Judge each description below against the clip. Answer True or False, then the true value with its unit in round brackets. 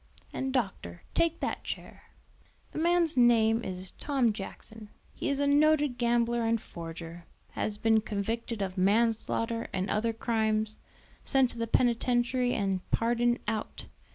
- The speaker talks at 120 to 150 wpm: True (140 wpm)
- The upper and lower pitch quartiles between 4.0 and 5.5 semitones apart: False (2.6 semitones)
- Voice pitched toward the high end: True (230 Hz)